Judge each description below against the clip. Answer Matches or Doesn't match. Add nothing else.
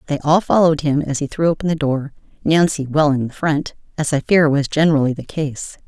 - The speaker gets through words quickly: Matches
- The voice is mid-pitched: Matches